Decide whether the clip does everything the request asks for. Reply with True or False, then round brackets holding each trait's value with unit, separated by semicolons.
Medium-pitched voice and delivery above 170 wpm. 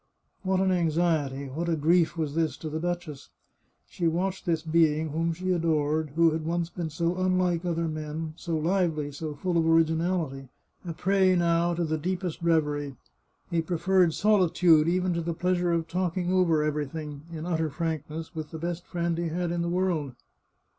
True (165 Hz; 180 wpm)